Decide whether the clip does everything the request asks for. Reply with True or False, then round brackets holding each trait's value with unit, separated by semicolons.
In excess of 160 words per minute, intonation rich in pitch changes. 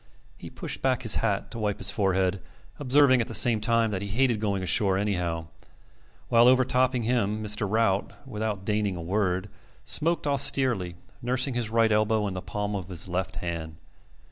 False (175 wpm; 4.1 semitones)